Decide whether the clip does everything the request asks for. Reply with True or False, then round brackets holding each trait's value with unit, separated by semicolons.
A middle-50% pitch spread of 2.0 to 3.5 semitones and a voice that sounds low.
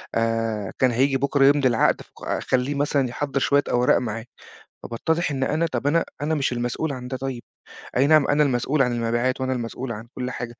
True (3.0 semitones; 130 Hz)